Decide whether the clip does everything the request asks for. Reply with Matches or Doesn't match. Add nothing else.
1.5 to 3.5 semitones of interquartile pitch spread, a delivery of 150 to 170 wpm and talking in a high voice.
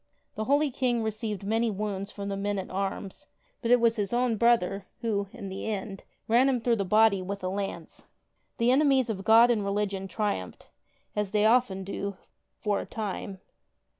Doesn't match